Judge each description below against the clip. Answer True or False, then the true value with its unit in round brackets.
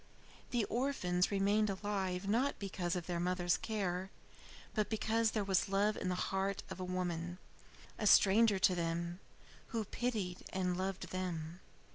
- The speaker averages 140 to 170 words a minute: True (150 wpm)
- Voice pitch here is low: False (190 Hz)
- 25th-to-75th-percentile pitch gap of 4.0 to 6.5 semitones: False (2.8 semitones)